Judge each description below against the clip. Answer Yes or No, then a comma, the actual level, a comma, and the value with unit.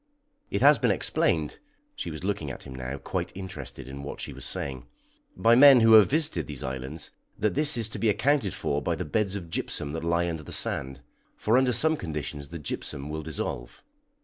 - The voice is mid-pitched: No, very low, 85 Hz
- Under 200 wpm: No, fast, 205 wpm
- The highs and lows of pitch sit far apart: Yes, wide, 7.7 semitones